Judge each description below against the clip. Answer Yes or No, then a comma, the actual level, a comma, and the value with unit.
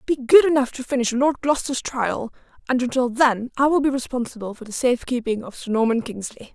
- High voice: Yes, very high, 250 Hz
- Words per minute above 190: Yes, average, 200 wpm